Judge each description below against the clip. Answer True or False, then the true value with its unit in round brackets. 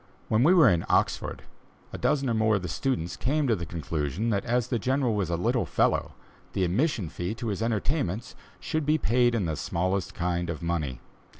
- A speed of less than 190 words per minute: False (205 wpm)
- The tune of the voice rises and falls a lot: True (6.2 semitones)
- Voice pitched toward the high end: False (105 Hz)